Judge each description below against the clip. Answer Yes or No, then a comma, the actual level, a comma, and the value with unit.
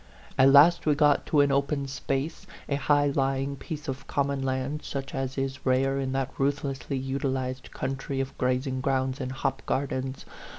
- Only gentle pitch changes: Yes, narrow, 1.1 semitones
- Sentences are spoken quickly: No, average, 170 wpm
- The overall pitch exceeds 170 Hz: No, low, 135 Hz